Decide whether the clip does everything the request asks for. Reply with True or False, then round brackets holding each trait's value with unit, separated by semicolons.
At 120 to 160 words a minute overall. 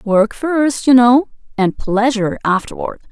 True (135 wpm)